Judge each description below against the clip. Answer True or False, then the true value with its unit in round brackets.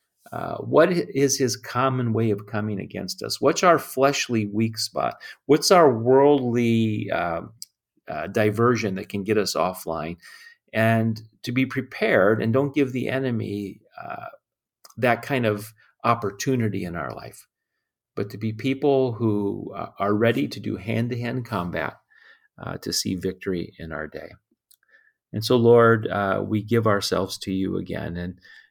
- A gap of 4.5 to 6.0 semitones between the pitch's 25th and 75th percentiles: False (3.6 semitones)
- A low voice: True (110 Hz)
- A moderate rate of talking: True (155 wpm)